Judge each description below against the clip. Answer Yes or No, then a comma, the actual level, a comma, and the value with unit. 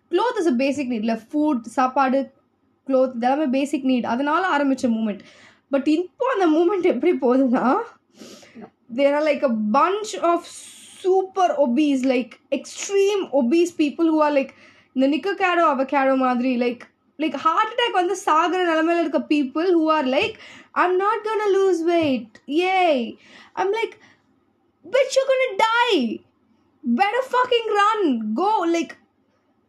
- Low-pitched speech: No, very high, 310 Hz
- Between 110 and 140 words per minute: Yes, slow, 135 wpm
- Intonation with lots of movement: Yes, wide, 5.8 semitones